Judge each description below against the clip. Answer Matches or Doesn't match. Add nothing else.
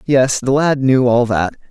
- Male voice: Matches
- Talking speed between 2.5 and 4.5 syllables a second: Matches